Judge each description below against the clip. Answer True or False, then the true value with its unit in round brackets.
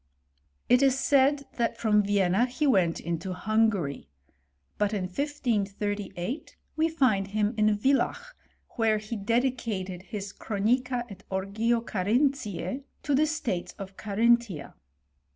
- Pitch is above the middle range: True (215 Hz)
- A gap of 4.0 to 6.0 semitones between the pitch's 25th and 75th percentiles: True (4.3 semitones)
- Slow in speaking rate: True (125 wpm)